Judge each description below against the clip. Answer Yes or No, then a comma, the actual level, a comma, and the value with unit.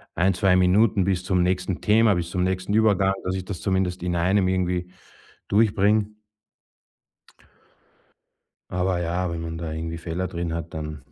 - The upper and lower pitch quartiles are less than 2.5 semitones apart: Yes, narrow, 1.9 semitones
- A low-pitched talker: Yes, very low, 90 Hz